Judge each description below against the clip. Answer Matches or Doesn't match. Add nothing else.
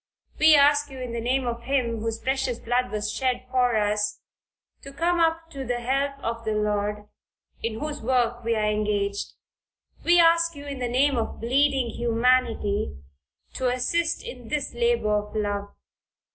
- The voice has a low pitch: Doesn't match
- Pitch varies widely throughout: Doesn't match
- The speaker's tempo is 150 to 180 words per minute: Matches